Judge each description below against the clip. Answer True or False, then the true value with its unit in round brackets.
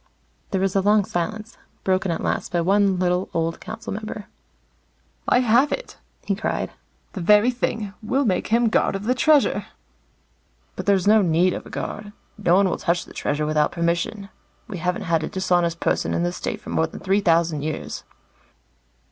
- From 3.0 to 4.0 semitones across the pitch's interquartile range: True (3.7 semitones)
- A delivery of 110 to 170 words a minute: False (185 wpm)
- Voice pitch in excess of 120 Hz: True (190 Hz)